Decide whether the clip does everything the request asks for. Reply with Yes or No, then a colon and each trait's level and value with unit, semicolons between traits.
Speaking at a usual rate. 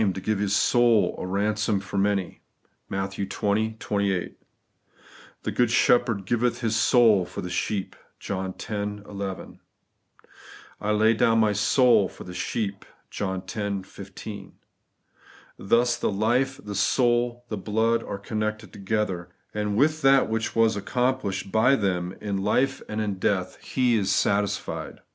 Yes: average, 145 wpm